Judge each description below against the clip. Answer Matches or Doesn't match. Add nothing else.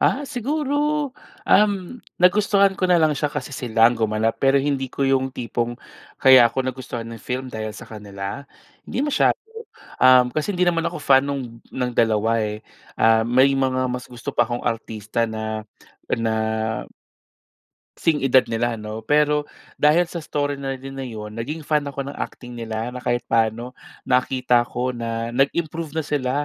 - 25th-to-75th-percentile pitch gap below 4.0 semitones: Doesn't match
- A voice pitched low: Matches